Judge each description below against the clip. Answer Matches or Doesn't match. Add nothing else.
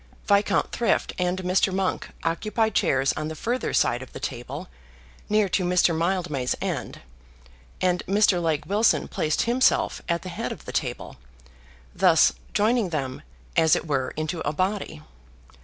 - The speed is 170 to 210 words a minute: Doesn't match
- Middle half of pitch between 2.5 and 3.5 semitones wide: Doesn't match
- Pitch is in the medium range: Matches